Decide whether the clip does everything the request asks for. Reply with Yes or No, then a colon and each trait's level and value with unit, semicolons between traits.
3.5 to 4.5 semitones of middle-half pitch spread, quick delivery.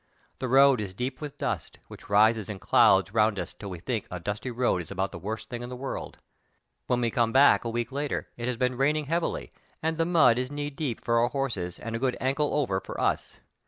Yes: average, 4.2 semitones; fast, 240 wpm